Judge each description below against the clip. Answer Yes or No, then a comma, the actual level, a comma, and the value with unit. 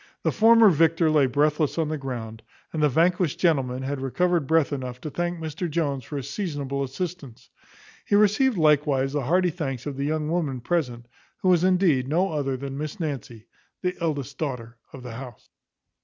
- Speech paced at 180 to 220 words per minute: Yes, average, 185 wpm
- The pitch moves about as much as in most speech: Yes, average, 4.2 semitones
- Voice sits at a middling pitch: Yes, medium, 150 Hz